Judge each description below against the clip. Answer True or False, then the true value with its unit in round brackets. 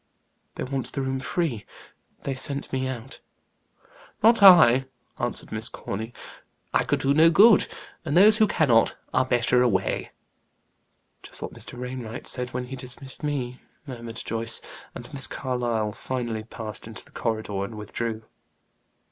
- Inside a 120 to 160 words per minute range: True (150 wpm)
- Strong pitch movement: False (3.0 semitones)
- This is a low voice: True (125 Hz)